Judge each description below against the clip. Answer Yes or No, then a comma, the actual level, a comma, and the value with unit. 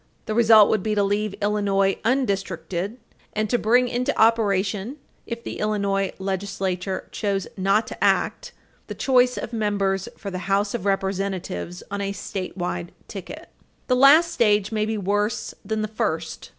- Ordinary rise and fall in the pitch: No, narrow, 2.2 semitones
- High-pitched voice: Yes, high, 205 Hz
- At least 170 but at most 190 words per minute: No, average, 155 wpm